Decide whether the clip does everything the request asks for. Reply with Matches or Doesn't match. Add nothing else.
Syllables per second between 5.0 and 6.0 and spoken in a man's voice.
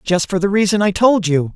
Matches